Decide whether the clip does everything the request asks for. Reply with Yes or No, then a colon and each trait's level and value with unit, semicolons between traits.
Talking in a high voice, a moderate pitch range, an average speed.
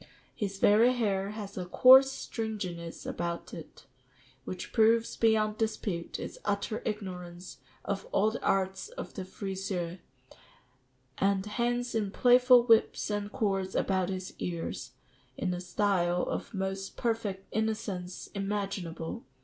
No: high, 200 Hz; average, 3.0 semitones; slow, 130 wpm